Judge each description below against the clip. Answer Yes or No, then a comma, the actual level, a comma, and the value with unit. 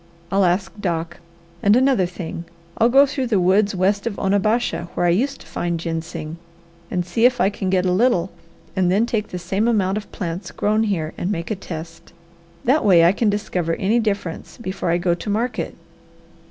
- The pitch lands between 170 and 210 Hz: Yes, high, 190 Hz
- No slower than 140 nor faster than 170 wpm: No, average, 195 wpm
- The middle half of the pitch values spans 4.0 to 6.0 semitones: No, average, 3.6 semitones